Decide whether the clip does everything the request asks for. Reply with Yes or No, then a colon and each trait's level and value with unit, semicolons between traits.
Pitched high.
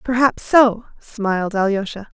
Yes: high, 220 Hz